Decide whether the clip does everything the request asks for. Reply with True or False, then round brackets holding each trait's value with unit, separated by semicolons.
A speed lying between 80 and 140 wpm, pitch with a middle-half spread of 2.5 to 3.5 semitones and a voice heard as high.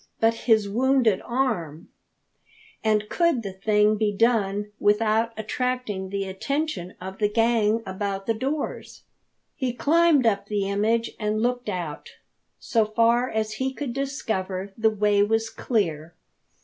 True (135 wpm; 3.2 semitones; 215 Hz)